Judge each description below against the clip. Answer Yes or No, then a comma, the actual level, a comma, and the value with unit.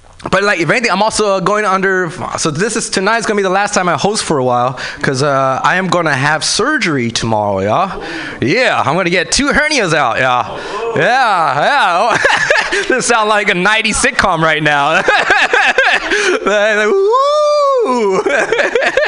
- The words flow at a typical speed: Yes, average, 160 wpm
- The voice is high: Yes, high, 195 Hz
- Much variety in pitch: Yes, wide, 6.7 semitones